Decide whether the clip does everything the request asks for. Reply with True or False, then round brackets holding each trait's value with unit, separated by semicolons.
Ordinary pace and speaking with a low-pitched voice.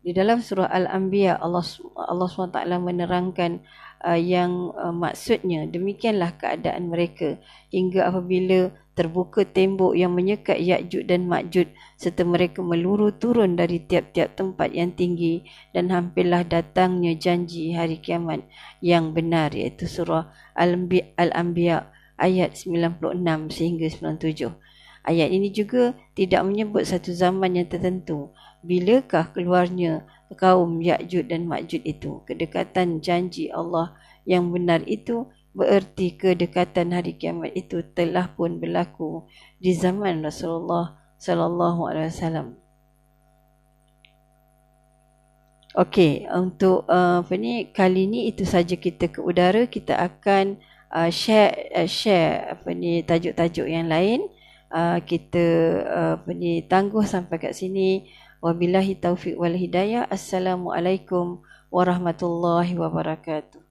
False (115 wpm; 175 Hz)